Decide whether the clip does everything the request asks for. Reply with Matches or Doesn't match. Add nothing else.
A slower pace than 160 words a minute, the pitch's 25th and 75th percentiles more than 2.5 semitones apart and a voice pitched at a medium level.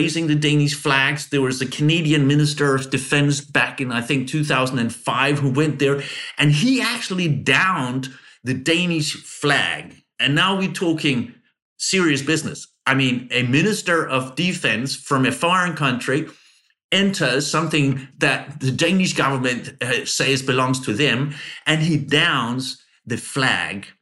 Matches